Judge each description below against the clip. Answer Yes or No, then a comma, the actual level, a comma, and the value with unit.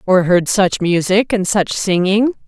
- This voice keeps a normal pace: Yes, average, 170 wpm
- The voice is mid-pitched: No, high, 195 Hz